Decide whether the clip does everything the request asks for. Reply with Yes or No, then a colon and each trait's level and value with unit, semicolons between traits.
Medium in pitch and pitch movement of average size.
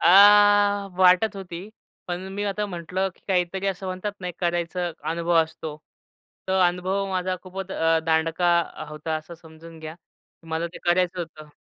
No: medium, 175 Hz; narrow, 2.3 semitones